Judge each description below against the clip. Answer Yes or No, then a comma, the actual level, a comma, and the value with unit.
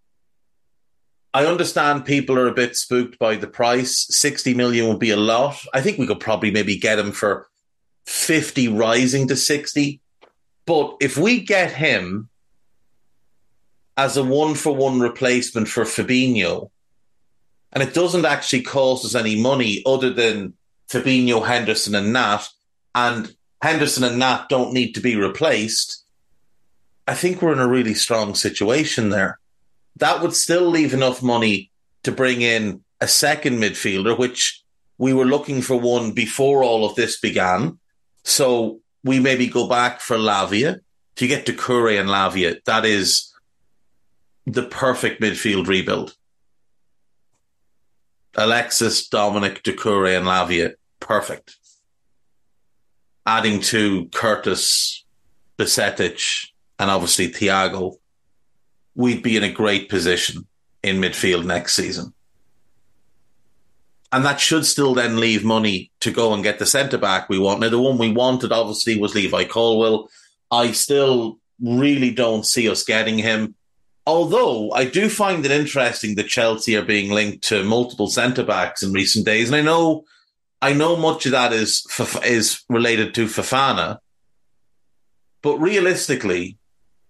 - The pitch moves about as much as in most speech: Yes, average, 3.9 semitones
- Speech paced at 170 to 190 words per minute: No, average, 140 wpm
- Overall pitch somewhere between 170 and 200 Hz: No, low, 115 Hz